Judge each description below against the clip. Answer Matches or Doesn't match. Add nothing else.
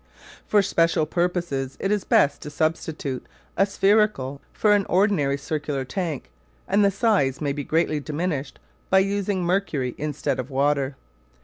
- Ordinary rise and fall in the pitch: Doesn't match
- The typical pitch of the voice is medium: Matches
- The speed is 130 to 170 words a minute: Matches